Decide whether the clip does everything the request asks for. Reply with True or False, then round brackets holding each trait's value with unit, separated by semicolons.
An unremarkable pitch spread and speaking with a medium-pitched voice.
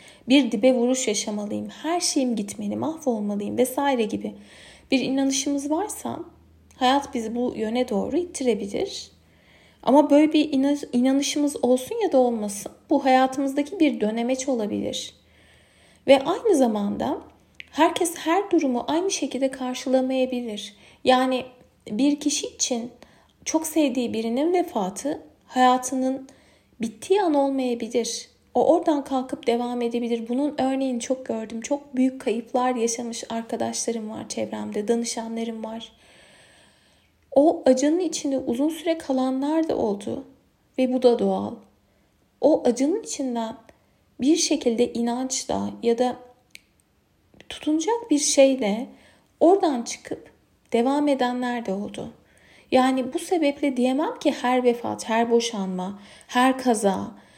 False (3.7 semitones; 255 Hz)